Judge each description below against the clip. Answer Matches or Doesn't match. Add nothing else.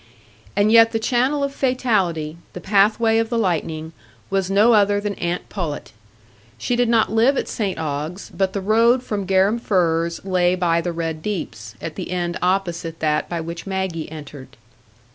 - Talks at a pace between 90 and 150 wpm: Doesn't match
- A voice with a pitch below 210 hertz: Matches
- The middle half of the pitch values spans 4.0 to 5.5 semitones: Matches